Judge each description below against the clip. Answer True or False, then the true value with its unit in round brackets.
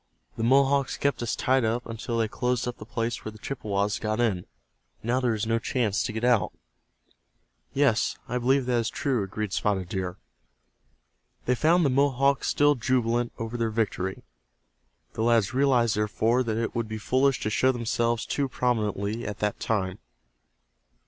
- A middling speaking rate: True (170 wpm)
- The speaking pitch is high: False (115 Hz)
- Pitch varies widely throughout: False (2.8 semitones)